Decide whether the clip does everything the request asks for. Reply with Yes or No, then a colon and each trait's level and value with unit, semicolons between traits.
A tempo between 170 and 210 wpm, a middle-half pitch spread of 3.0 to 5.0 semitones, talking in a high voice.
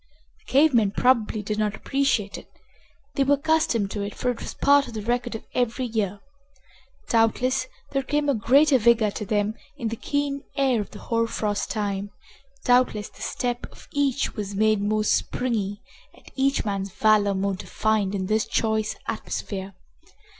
Yes: average, 175 wpm; average, 3.8 semitones; high, 225 Hz